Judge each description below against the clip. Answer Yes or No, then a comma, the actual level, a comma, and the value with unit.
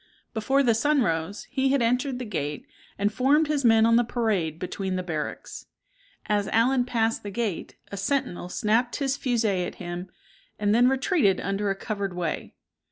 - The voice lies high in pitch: Yes, high, 220 Hz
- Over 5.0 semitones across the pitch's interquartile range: No, average, 4.6 semitones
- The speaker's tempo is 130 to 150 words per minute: No, average, 175 wpm